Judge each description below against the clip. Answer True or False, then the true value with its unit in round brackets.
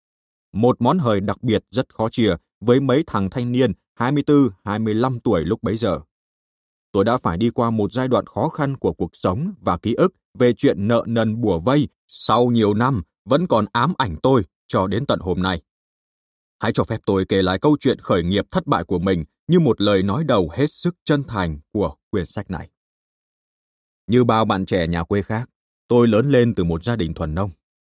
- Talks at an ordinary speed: True (205 wpm)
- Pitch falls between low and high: False (110 Hz)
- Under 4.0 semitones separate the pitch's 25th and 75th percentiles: False (4.6 semitones)